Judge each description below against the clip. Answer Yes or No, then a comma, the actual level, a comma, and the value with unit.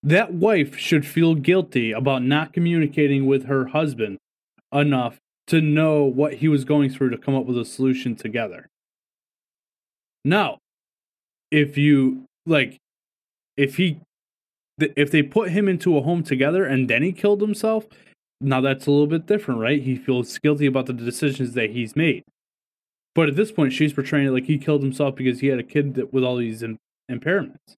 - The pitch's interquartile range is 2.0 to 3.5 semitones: Yes, average, 3.1 semitones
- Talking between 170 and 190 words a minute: Yes, average, 180 wpm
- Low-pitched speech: No, medium, 145 Hz